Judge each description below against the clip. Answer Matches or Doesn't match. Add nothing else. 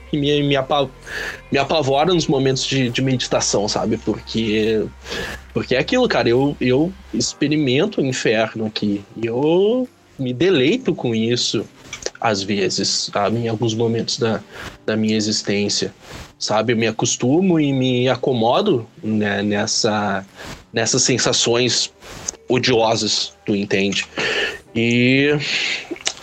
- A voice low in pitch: Matches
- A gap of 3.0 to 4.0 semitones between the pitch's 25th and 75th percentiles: Doesn't match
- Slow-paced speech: Matches